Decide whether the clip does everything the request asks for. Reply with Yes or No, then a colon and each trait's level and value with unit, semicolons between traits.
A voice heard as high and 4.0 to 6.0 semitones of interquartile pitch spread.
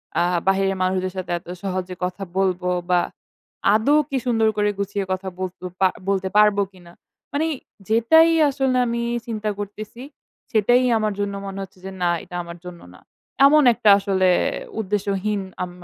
No: high, 200 Hz; average, 2.9 semitones